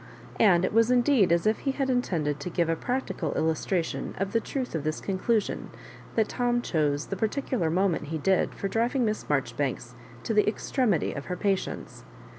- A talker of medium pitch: No, high, 195 Hz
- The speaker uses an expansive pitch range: Yes, wide, 6.4 semitones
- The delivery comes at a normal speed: Yes, average, 195 wpm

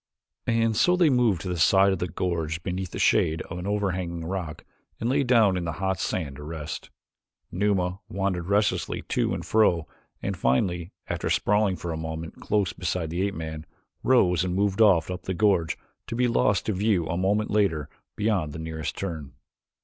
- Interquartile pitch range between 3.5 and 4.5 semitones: Yes, average, 3.8 semitones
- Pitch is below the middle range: Yes, very low, 90 Hz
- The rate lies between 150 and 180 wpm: No, average, 190 wpm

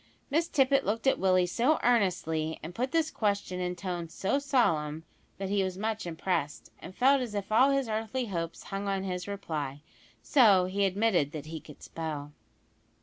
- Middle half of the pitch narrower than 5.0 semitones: No, wide, 5.4 semitones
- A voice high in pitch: Yes, high, 195 Hz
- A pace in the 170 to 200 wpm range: Yes, average, 180 wpm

